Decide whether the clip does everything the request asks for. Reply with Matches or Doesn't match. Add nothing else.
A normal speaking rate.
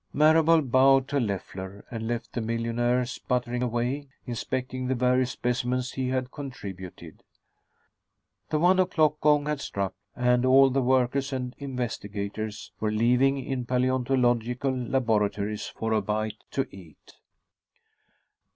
Doesn't match